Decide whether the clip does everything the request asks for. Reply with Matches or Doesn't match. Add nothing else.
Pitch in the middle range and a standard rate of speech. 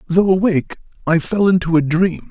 Matches